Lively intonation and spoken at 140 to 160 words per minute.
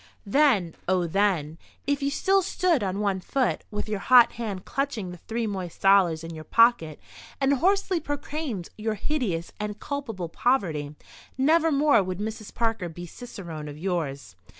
Yes: wide, 7.6 semitones; average, 150 wpm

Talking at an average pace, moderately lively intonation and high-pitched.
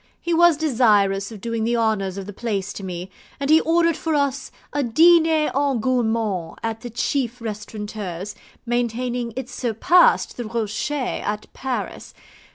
Yes: average, 155 wpm; average, 4.9 semitones; high, 235 Hz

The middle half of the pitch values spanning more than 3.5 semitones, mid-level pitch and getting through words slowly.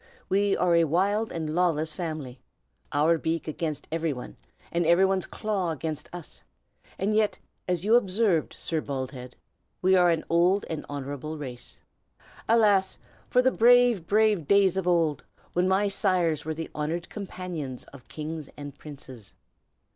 No: average, 4.1 semitones; medium, 170 Hz; average, 155 wpm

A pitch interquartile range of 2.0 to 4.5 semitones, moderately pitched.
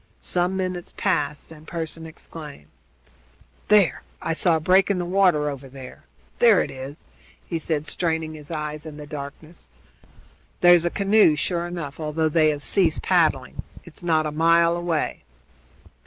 Yes: average, 2.7 semitones; medium, 160 Hz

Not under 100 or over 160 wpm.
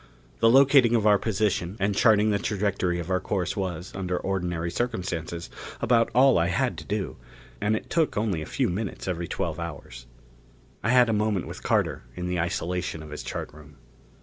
No: average, 190 wpm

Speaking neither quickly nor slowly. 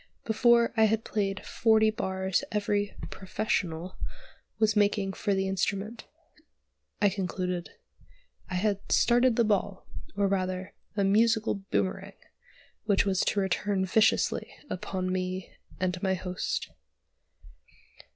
No: slow, 115 wpm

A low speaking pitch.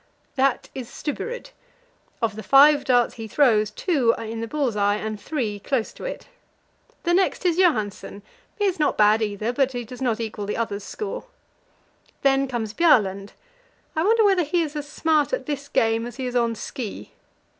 No: very high, 250 Hz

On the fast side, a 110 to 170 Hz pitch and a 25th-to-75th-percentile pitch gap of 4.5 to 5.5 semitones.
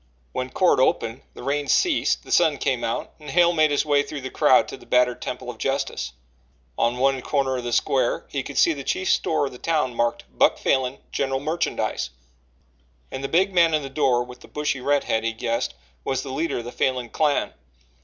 No: fast, 215 wpm; low, 135 Hz; average, 3.2 semitones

